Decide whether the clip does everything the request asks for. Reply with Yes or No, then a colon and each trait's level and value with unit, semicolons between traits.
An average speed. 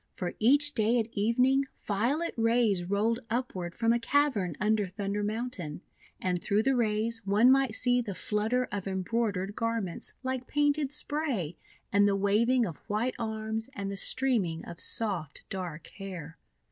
Yes: average, 160 wpm